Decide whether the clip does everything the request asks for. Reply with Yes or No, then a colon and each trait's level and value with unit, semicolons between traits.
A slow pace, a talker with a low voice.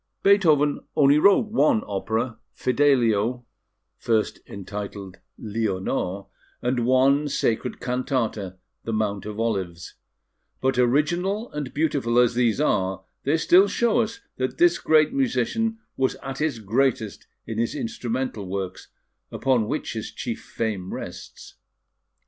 Yes: slow, 125 wpm; low, 125 Hz